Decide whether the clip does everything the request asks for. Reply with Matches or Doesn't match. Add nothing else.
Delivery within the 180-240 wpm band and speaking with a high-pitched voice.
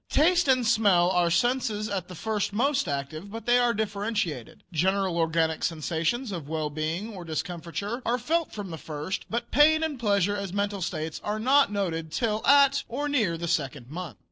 Matches